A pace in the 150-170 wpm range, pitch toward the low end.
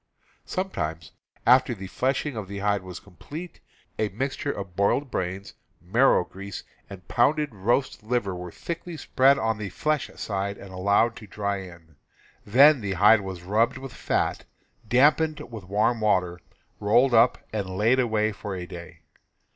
Yes: average, 155 wpm; low, 105 Hz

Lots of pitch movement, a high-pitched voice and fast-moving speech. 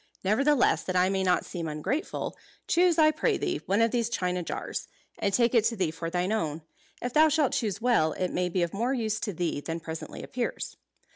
Yes: wide, 5.8 semitones; high, 200 Hz; fast, 215 wpm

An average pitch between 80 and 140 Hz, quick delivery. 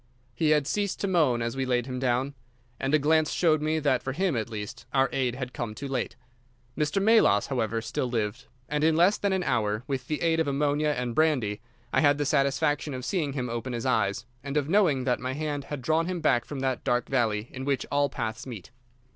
Yes: low, 135 Hz; fast, 230 wpm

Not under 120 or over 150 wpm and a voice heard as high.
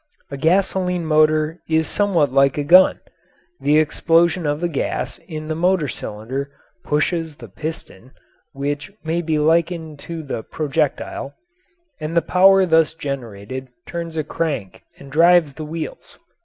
No: average, 140 wpm; medium, 155 Hz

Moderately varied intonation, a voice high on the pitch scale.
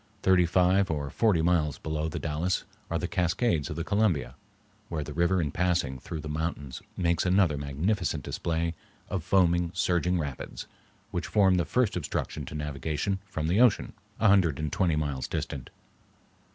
No: average, 3.5 semitones; very low, 85 Hz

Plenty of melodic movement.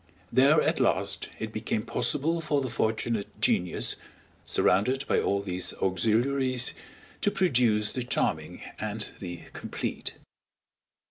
No: average, 4.7 semitones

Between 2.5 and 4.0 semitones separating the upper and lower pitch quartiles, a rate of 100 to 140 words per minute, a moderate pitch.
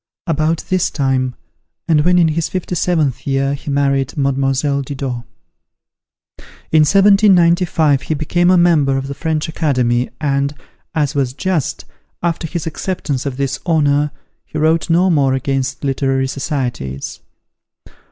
Yes: average, 3.4 semitones; slow, 135 wpm; medium, 145 Hz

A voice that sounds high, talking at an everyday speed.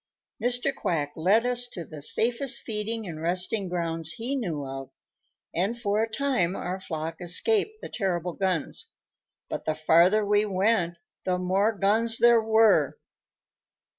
Yes: high, 195 Hz; average, 145 wpm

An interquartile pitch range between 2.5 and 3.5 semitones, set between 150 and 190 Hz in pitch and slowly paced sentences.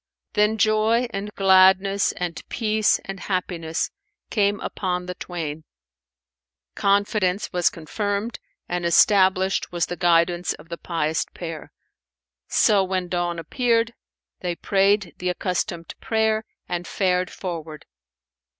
Yes: average, 2.8 semitones; medium, 185 Hz; slow, 115 wpm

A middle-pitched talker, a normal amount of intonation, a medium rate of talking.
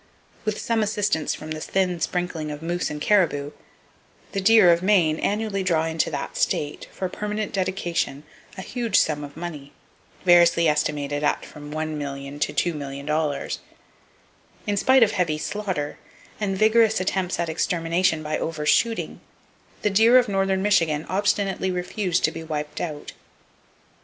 Yes: medium, 175 Hz; average, 4.6 semitones; average, 145 wpm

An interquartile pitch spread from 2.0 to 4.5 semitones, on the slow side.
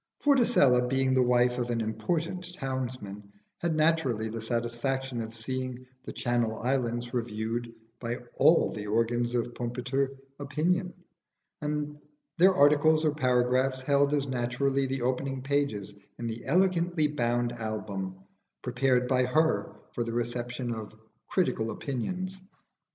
Yes: average, 3.3 semitones; slow, 130 wpm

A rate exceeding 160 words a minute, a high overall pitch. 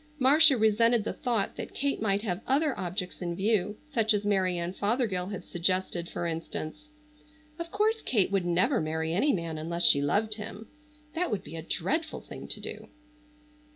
Yes: average, 180 wpm; high, 200 Hz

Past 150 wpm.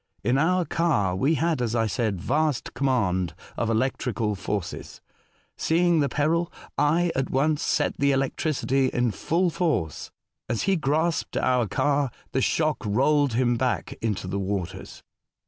No: average, 145 wpm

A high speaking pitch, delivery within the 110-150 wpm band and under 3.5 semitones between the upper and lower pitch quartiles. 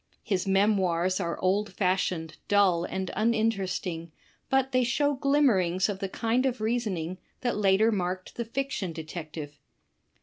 No: high, 195 Hz; average, 140 wpm; average, 4.2 semitones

